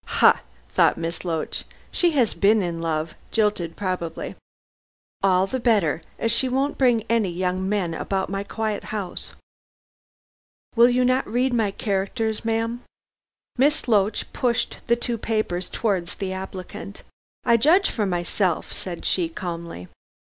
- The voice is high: Yes, high, 205 Hz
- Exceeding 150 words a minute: No, average, 140 wpm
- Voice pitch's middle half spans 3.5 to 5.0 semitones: Yes, average, 4.4 semitones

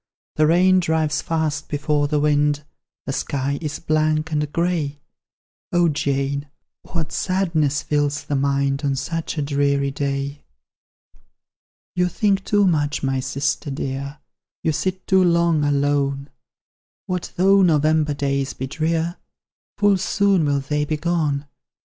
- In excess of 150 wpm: No, slow, 135 wpm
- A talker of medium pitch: Yes, medium, 150 Hz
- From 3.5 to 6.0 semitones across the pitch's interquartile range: No, average, 3.0 semitones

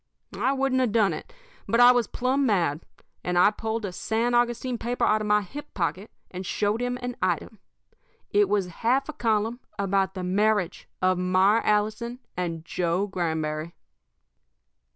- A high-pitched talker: Yes, high, 210 Hz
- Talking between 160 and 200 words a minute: Yes, average, 165 wpm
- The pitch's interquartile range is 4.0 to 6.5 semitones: Yes, average, 4.6 semitones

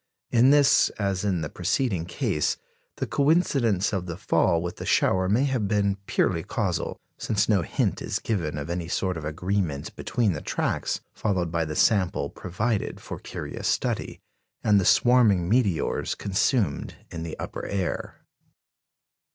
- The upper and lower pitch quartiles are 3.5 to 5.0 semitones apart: Yes, average, 4.3 semitones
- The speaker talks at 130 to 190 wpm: Yes, average, 155 wpm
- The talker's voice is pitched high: No, very low, 95 Hz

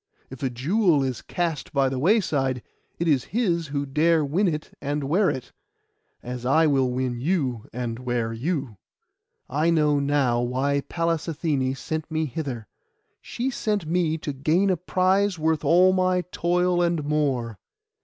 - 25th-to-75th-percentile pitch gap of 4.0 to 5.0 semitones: Yes, average, 4.6 semitones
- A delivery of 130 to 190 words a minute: Yes, average, 165 wpm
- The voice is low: No, medium, 150 Hz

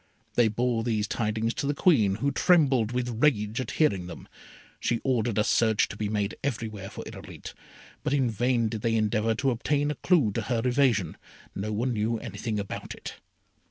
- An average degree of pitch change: Yes, average, 3.2 semitones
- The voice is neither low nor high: No, low, 115 Hz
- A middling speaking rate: Yes, average, 190 wpm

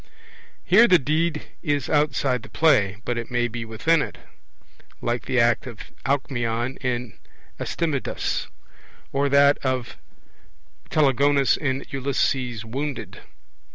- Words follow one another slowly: Yes, slow, 125 wpm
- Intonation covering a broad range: No, average, 3.2 semitones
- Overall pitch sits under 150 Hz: Yes, low, 135 Hz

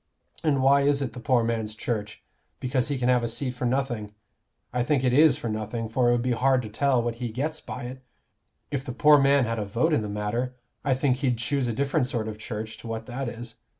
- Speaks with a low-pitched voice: Yes, low, 125 Hz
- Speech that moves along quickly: Yes, fast, 250 wpm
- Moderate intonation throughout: Yes, average, 3.0 semitones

